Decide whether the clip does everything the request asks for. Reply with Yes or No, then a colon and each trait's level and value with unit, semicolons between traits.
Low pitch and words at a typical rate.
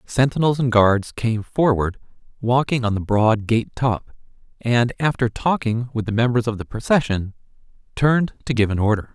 Yes: low, 115 Hz; average, 165 wpm